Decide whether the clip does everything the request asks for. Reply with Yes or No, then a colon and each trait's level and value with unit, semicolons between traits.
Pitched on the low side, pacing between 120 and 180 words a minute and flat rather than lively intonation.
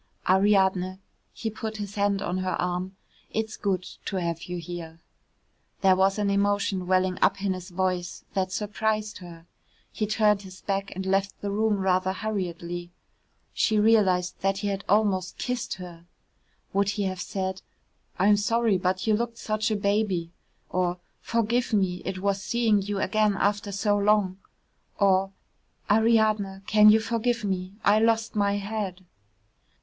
No: high, 200 Hz; average, 155 wpm; narrow, 2.2 semitones